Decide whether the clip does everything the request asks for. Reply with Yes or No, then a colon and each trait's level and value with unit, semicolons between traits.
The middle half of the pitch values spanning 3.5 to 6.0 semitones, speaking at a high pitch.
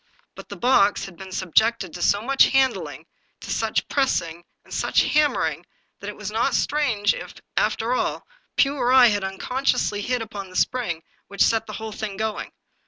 Yes: average, 4.5 semitones; high, 220 Hz